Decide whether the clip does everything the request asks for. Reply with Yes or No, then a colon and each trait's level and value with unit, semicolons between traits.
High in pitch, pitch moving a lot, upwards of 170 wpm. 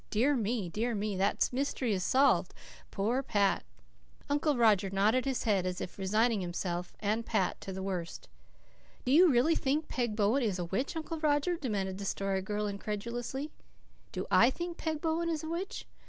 Yes: high, 225 Hz; wide, 6.2 semitones; average, 180 wpm